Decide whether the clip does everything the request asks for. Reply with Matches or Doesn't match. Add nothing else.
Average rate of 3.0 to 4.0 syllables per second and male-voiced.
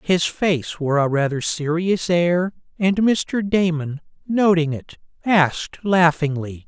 Matches